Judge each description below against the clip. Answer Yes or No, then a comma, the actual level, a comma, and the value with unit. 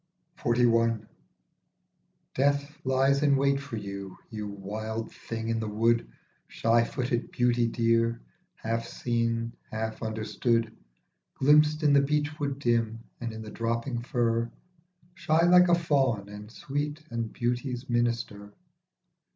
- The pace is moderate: No, slow, 130 wpm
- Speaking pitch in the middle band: No, low, 115 Hz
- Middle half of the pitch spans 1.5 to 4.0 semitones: Yes, average, 3.6 semitones